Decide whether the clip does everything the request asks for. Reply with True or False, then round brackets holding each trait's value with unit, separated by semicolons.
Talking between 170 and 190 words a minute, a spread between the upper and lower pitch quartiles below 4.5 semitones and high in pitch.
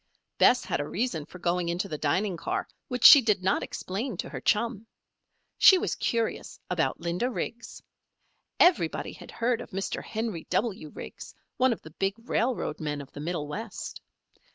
False (175 wpm; 5.6 semitones; 195 Hz)